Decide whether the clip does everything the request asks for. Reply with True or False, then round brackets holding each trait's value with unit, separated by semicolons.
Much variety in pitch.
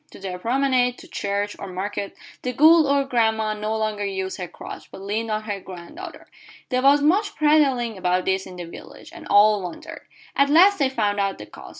True (5.7 semitones)